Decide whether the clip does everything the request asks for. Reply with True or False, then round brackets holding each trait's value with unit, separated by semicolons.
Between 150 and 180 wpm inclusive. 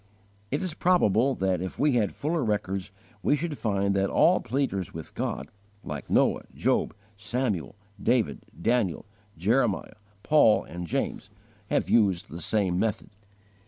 False (140 wpm)